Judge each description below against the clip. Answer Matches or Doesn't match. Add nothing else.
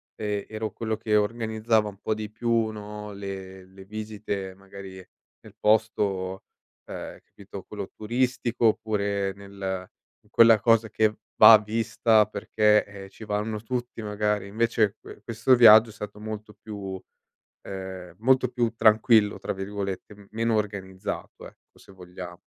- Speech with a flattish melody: Matches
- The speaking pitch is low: Matches